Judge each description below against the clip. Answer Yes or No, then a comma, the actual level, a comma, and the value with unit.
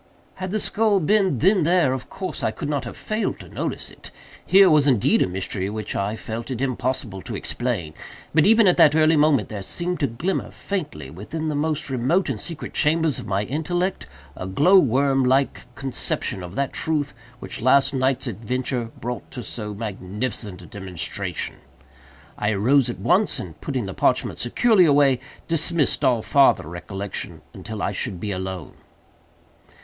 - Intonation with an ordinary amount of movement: No, wide, 7.0 semitones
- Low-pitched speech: Yes, low, 130 Hz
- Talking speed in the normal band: Yes, average, 175 wpm